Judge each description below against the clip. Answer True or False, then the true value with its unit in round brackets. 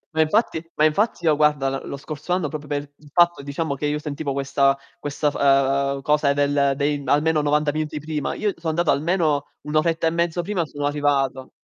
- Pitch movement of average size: False (2.0 semitones)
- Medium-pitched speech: True (150 Hz)